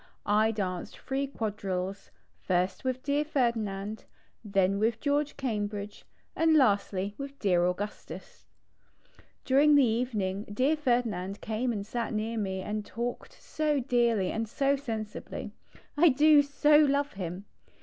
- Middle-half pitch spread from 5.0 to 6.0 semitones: Yes, wide, 5.5 semitones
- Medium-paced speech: No, slow, 130 wpm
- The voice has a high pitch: Yes, high, 225 Hz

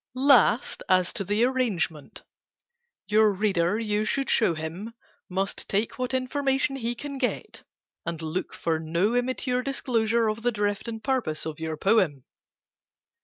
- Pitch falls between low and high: No, high, 215 Hz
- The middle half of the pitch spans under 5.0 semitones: No, wide, 5.6 semitones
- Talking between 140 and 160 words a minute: Yes, average, 150 wpm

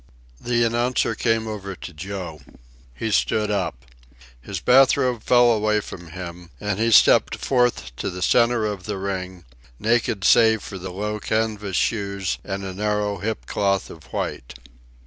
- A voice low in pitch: Yes, low, 105 Hz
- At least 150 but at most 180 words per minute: Yes, average, 160 wpm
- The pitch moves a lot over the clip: No, average, 3.1 semitones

